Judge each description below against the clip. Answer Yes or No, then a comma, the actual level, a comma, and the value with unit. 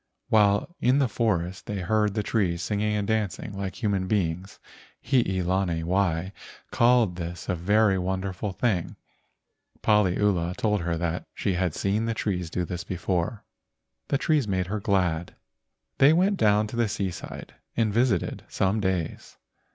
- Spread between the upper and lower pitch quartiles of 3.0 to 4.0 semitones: Yes, average, 3.3 semitones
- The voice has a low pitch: Yes, low, 100 Hz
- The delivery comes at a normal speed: Yes, average, 150 wpm